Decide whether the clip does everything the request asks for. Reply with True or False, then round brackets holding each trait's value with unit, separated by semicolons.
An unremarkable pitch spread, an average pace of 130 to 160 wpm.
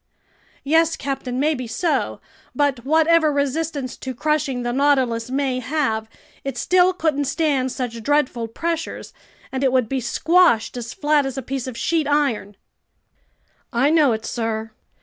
True (3.8 semitones; 150 wpm)